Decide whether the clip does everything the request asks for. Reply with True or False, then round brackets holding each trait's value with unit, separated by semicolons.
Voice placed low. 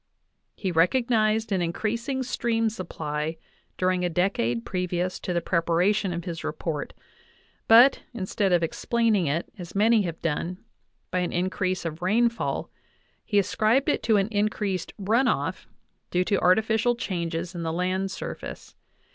False (185 Hz)